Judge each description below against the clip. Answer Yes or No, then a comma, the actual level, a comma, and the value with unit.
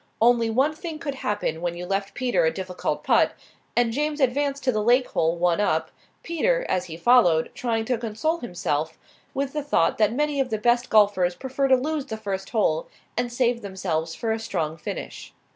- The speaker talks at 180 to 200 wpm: Yes, average, 195 wpm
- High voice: Yes, high, 225 Hz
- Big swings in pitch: Yes, wide, 6.4 semitones